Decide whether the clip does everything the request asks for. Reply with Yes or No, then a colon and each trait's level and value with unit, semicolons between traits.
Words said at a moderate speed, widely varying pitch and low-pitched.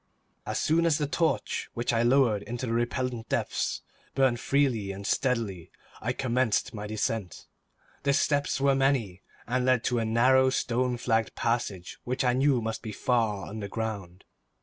No: average, 160 wpm; average, 3.1 semitones; low, 120 Hz